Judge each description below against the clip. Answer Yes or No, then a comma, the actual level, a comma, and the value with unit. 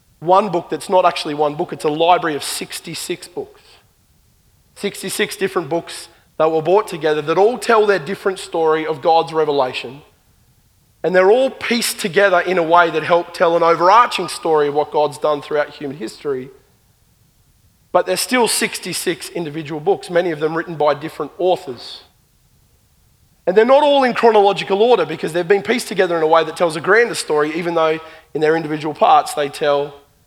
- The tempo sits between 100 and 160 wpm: No, average, 180 wpm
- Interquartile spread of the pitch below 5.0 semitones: Yes, average, 4.3 semitones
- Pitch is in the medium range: Yes, medium, 170 Hz